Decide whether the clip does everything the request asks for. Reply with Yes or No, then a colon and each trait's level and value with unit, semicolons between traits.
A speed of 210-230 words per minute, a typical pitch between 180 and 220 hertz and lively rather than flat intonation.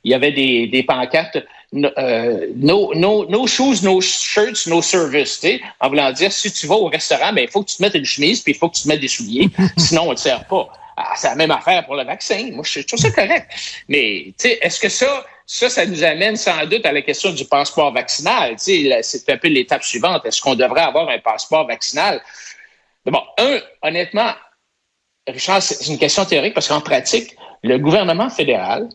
Yes: average, 215 wpm; high, 190 Hz; wide, 6.7 semitones